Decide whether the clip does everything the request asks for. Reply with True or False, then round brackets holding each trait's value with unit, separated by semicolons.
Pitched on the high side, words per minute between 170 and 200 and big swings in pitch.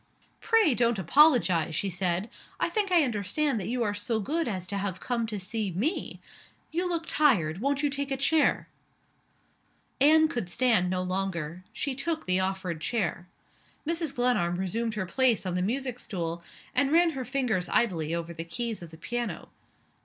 True (225 Hz; 175 wpm; 7.1 semitones)